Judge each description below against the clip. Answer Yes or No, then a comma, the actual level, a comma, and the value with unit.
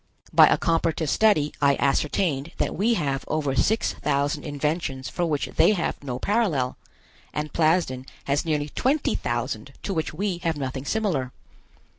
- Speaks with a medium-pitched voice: Yes, medium, 150 Hz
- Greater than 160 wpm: No, average, 155 wpm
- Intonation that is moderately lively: Yes, average, 4.2 semitones